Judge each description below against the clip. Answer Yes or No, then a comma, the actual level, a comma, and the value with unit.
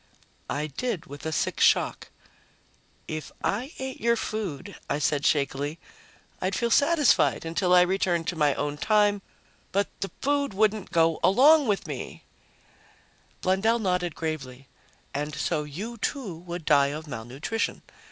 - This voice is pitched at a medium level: Yes, medium, 180 Hz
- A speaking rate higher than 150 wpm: No, average, 145 wpm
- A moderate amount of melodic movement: No, wide, 6.3 semitones